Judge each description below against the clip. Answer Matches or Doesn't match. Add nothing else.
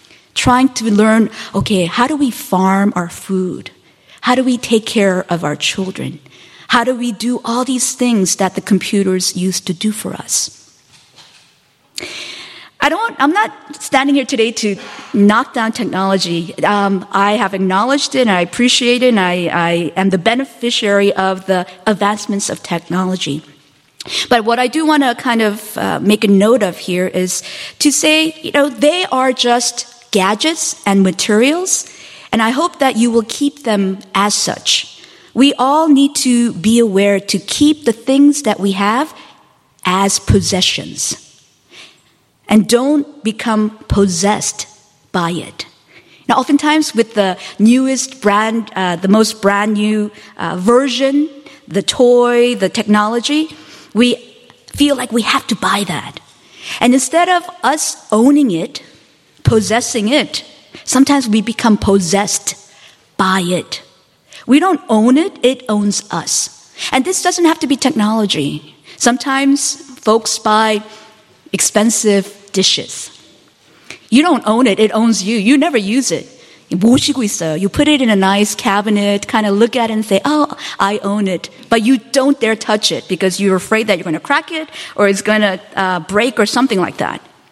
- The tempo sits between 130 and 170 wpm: Matches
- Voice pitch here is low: Doesn't match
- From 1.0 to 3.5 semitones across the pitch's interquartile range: Doesn't match